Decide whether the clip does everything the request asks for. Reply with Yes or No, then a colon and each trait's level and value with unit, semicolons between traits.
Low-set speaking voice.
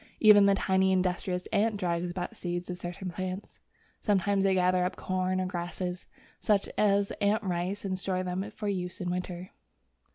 No: medium, 185 Hz